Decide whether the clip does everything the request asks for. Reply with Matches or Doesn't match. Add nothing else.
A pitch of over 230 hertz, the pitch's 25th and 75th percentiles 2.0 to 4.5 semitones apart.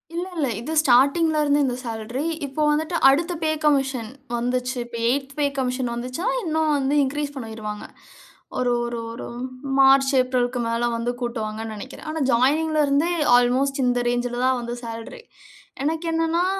Matches